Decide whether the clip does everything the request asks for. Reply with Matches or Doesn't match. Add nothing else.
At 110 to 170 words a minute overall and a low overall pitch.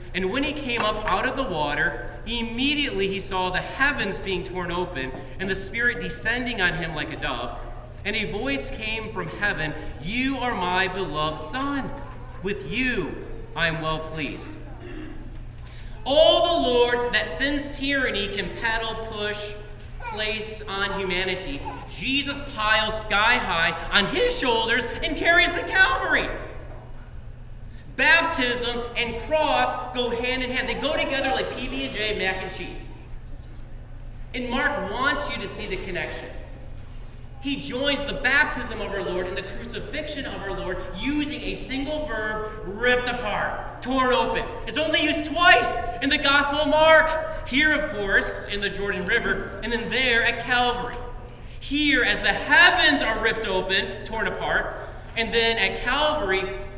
Doesn't match